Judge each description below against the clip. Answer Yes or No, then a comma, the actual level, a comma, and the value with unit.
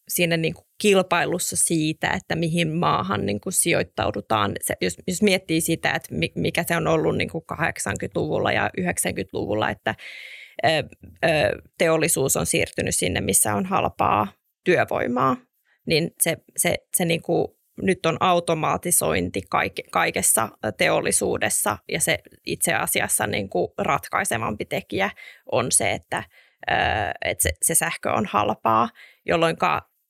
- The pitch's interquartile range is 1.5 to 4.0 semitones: Yes, narrow, 2.6 semitones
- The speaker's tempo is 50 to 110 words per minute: No, average, 135 wpm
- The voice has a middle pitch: Yes, medium, 170 Hz